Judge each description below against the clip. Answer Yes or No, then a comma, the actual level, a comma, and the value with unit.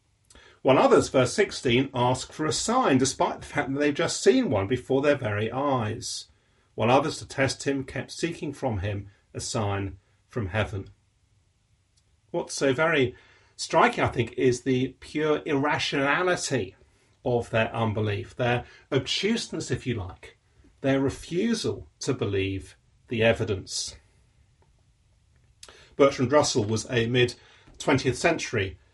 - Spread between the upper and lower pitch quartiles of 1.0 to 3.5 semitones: No, average, 4.6 semitones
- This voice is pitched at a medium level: No, low, 125 Hz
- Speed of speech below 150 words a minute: Yes, slow, 135 wpm